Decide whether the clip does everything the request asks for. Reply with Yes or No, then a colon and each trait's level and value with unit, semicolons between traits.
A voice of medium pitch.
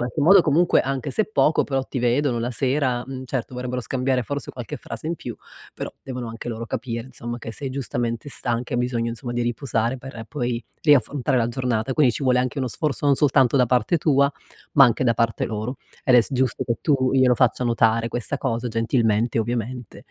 No: low, 125 Hz